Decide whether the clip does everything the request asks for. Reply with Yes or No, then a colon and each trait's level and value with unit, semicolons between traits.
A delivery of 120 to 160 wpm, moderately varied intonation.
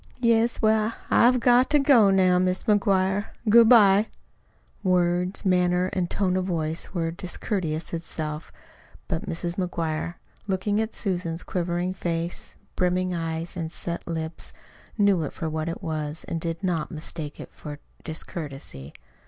Yes: average, 145 wpm; average, 3.2 semitones